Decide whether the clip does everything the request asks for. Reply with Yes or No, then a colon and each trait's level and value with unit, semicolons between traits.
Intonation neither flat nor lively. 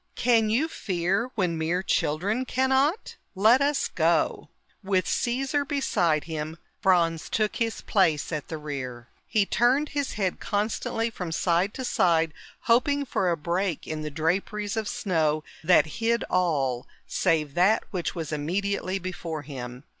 No: wide, 6.1 semitones